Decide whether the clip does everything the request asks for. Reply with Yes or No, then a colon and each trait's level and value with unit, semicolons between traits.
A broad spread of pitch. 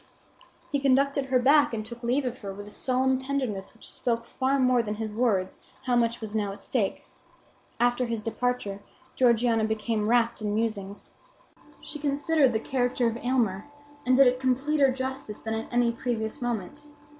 No: average, 3.0 semitones